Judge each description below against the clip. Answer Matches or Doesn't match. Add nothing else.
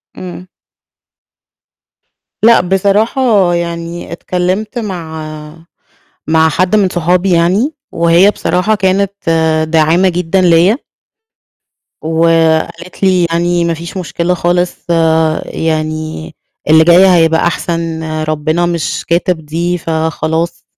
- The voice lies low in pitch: Doesn't match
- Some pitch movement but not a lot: Doesn't match